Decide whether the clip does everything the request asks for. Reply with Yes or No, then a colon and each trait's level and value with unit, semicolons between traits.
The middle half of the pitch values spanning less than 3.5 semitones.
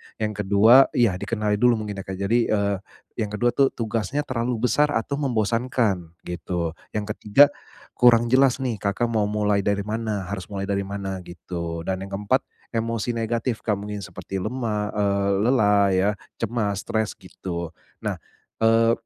Yes: average, 2.8 semitones